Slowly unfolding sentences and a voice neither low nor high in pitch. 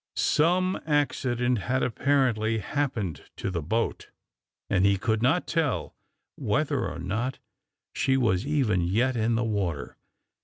No: slow, 130 wpm; low, 115 Hz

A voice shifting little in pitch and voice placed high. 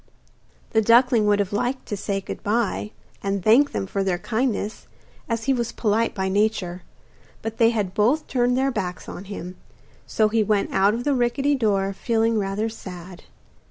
No: average, 3.2 semitones; high, 215 Hz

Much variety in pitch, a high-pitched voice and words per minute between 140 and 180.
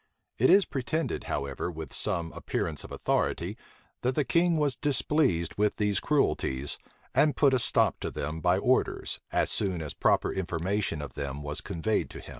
No: wide, 9.0 semitones; very low, 95 Hz; average, 175 wpm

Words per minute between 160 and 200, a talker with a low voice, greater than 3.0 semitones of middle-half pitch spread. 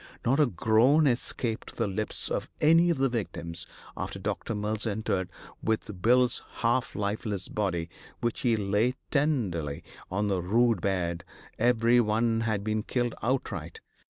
No: average, 145 wpm; low, 110 Hz; average, 3.6 semitones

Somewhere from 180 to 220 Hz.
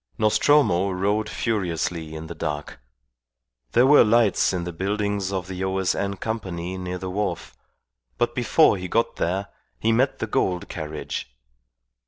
No: very low, 95 Hz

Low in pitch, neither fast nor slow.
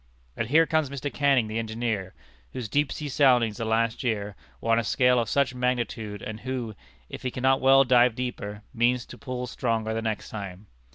Yes: low, 120 Hz; average, 195 wpm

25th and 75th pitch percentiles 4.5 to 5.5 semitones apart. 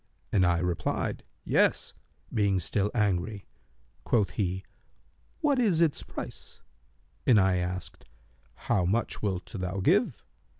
No: average, 3.1 semitones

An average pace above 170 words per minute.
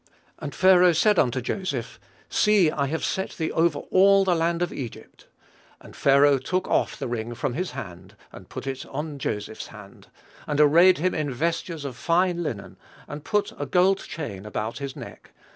Yes: average, 180 wpm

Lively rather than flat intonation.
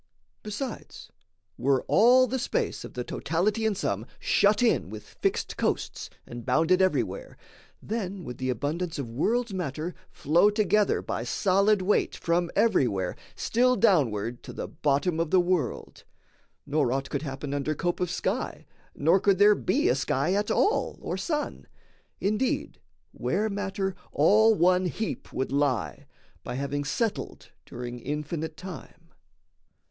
Yes: wide, 6.8 semitones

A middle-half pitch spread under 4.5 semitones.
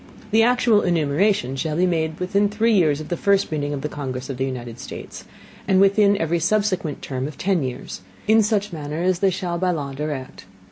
No: wide, 5.6 semitones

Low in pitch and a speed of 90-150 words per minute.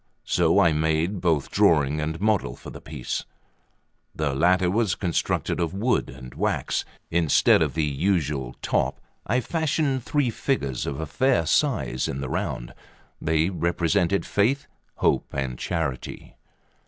Yes: very low, 85 Hz; average, 140 wpm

